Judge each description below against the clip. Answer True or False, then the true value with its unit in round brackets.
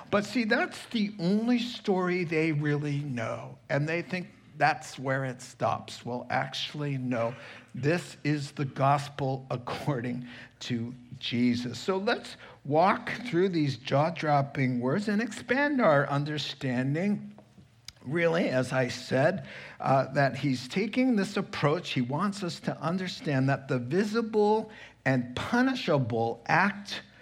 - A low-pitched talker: False (145 Hz)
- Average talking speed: False (130 wpm)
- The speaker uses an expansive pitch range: True (6.6 semitones)